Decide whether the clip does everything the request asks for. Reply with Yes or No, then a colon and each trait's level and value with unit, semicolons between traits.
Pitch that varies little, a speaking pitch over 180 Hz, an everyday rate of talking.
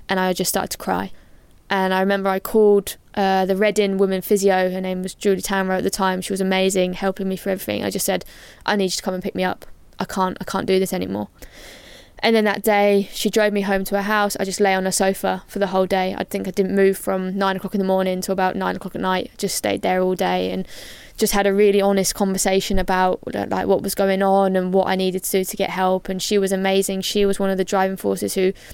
No: narrow, 1.0 semitones; high, 190 Hz; fast, 265 wpm